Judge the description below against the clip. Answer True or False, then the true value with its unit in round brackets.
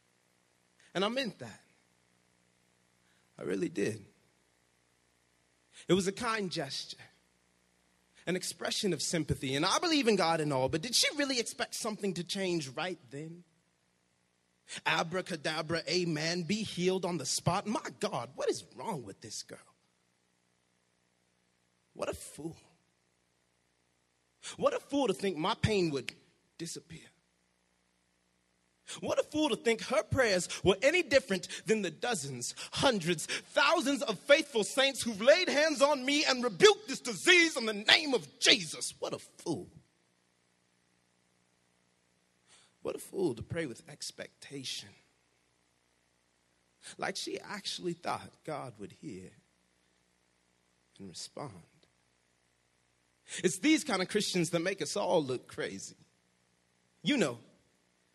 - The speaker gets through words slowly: True (130 wpm)